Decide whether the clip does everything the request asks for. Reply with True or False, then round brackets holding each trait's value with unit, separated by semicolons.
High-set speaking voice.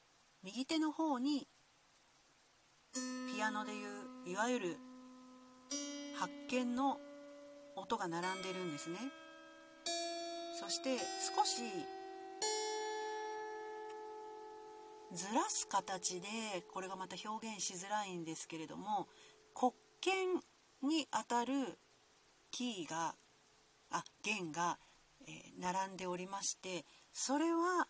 True (260 Hz)